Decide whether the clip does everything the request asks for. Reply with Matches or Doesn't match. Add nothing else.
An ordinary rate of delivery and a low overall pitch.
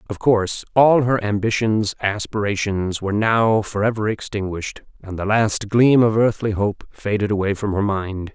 Matches